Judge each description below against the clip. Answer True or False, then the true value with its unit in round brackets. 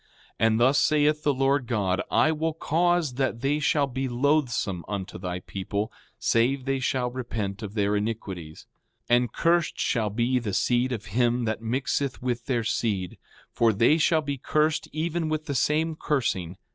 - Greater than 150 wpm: True (175 wpm)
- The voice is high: False (125 Hz)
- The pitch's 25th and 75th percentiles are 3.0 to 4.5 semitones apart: False (5.3 semitones)